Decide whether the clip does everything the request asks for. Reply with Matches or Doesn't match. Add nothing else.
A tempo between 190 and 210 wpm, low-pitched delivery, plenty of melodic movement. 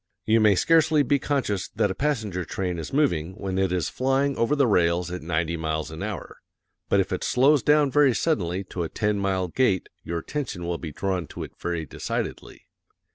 Matches